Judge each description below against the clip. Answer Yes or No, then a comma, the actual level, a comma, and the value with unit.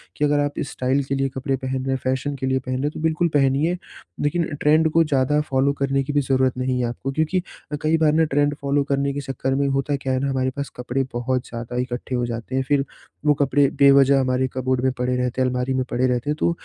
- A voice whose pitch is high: No, low, 135 Hz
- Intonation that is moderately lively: No, narrow, 1.9 semitones